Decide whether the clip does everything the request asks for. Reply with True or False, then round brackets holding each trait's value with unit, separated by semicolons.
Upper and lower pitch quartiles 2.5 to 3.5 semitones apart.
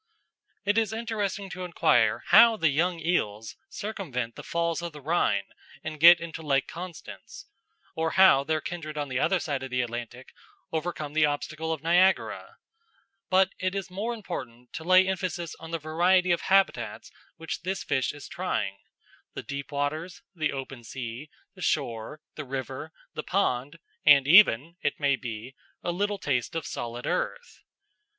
False (5.1 semitones)